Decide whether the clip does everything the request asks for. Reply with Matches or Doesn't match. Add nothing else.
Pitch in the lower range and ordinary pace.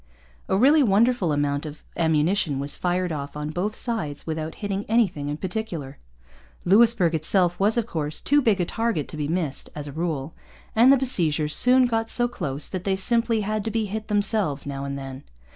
Doesn't match